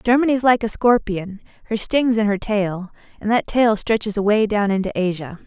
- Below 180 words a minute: No, average, 185 wpm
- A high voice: Yes, high, 215 Hz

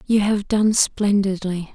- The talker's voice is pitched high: Yes, high, 200 Hz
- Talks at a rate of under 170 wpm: Yes, average, 140 wpm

